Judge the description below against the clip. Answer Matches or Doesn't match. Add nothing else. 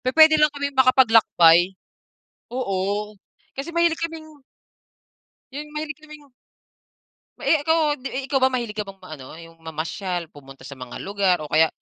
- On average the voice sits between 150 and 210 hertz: Doesn't match